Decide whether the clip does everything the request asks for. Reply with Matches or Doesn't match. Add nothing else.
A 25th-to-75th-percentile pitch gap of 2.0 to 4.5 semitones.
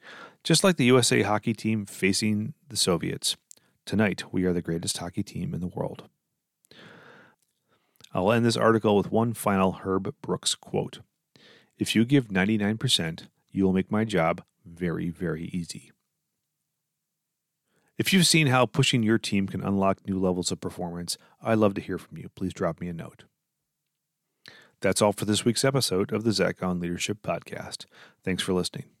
Doesn't match